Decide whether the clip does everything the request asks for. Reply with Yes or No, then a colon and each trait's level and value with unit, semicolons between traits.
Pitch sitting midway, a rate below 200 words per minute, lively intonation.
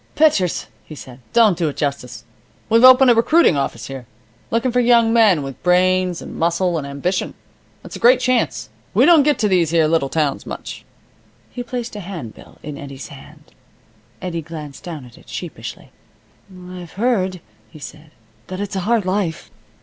Yes: medium, 180 Hz; average, 175 wpm; wide, 7.1 semitones